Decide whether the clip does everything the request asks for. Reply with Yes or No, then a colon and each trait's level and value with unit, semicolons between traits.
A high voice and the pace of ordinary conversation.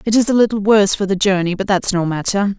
No: high, 200 Hz; fast, 280 wpm